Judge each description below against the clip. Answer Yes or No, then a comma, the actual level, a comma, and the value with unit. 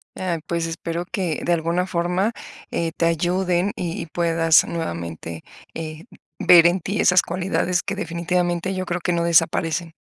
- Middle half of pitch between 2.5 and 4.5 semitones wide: No, narrow, 1.5 semitones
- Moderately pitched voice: Yes, medium, 170 Hz